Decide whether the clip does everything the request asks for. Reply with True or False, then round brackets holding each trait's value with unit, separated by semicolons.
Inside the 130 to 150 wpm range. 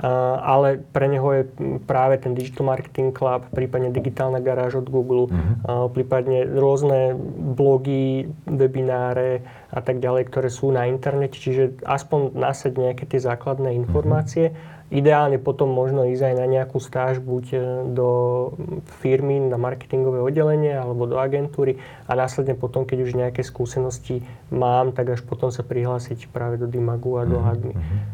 True (145 wpm)